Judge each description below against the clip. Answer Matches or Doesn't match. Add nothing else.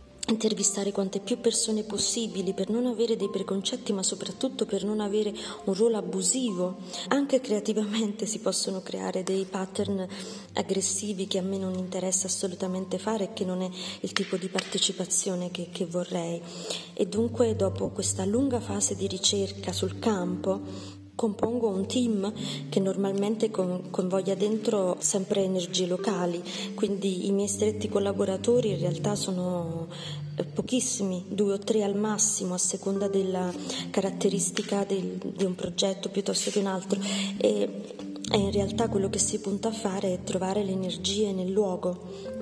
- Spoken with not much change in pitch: Matches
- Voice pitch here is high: Matches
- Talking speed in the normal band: Matches